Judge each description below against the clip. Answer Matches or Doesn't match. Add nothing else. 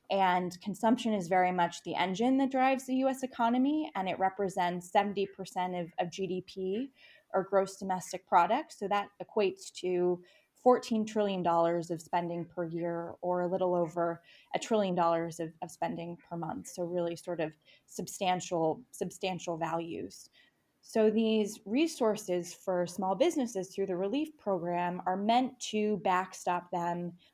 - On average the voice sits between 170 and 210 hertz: Matches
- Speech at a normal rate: Matches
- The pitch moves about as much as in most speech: Matches